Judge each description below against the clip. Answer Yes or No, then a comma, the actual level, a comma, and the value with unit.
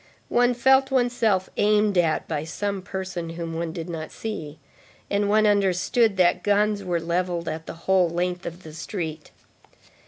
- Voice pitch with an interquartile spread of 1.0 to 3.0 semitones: No, average, 3.7 semitones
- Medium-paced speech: Yes, average, 160 wpm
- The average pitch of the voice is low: No, medium, 185 Hz